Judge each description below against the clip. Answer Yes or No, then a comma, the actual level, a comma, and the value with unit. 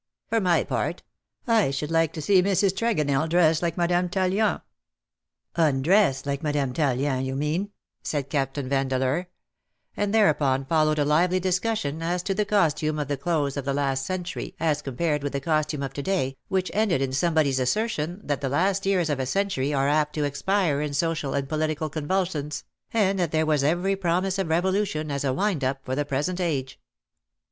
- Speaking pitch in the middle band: Yes, medium, 155 Hz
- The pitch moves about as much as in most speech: Yes, average, 4.6 semitones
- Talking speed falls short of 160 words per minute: No, average, 190 wpm